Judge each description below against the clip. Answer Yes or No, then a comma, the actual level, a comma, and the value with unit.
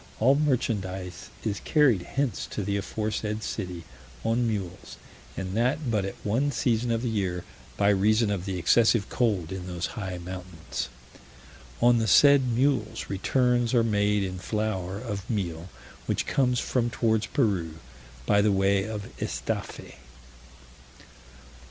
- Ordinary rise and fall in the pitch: Yes, average, 3.8 semitones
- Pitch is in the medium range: No, low, 105 Hz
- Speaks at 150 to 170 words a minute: No, average, 140 wpm